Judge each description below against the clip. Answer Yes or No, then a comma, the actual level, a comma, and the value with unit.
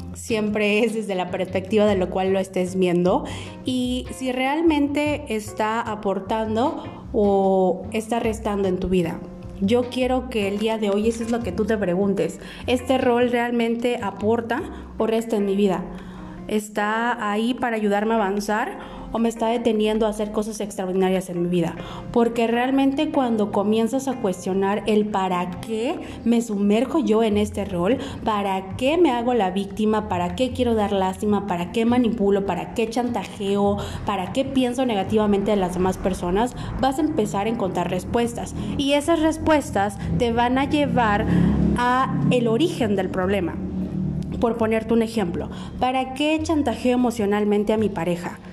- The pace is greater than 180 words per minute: No, average, 160 wpm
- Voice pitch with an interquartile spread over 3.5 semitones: Yes, average, 3.9 semitones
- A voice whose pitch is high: Yes, high, 215 Hz